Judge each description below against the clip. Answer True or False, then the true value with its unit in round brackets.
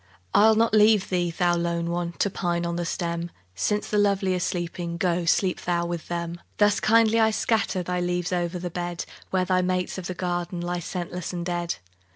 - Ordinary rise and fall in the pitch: False (1.6 semitones)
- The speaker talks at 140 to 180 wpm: False (200 wpm)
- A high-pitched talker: False (175 Hz)